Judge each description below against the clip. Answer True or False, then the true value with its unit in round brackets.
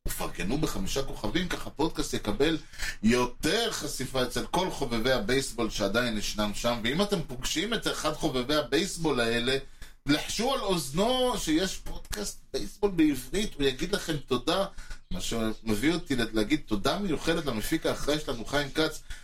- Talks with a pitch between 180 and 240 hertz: False (140 Hz)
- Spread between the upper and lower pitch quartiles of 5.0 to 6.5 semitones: True (5.4 semitones)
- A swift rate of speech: False (140 wpm)